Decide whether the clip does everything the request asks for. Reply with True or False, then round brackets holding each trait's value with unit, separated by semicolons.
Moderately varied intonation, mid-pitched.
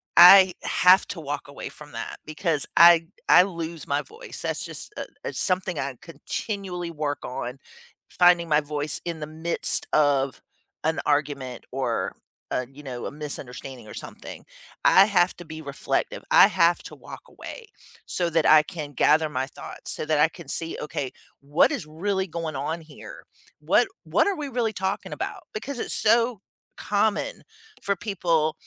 True (3.9 semitones; 160 Hz)